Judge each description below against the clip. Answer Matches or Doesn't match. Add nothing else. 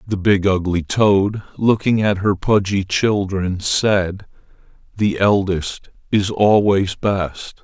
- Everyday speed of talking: Doesn't match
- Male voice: Matches